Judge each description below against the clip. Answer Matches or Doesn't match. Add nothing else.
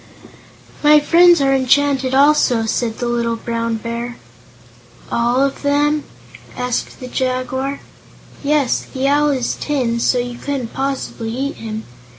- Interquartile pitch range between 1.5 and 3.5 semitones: Matches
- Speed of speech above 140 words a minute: Doesn't match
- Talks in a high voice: Matches